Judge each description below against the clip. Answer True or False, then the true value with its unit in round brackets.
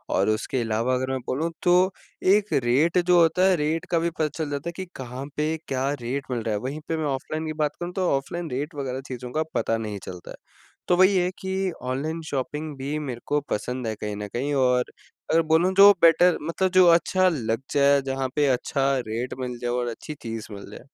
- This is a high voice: False (140 Hz)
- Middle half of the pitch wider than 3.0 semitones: True (4.9 semitones)